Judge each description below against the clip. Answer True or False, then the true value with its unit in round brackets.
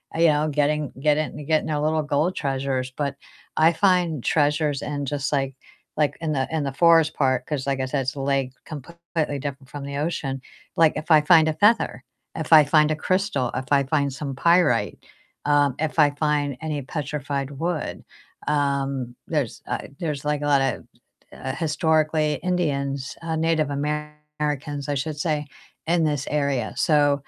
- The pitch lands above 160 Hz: False (150 Hz)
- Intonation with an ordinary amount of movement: False (2.1 semitones)